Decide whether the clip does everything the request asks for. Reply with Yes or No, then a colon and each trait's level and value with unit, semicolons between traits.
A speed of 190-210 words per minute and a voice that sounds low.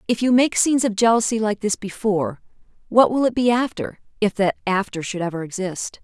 No: average, 200 wpm; high, 215 Hz